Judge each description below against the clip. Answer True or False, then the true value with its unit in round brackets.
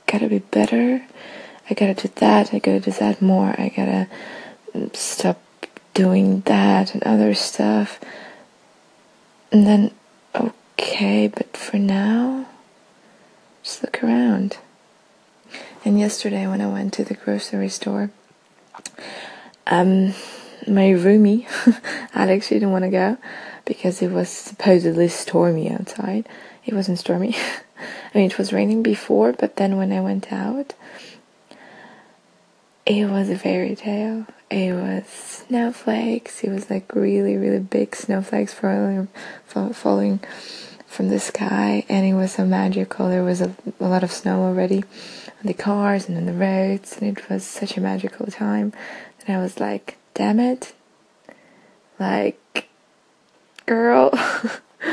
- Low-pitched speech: False (195 Hz)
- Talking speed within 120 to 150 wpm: True (135 wpm)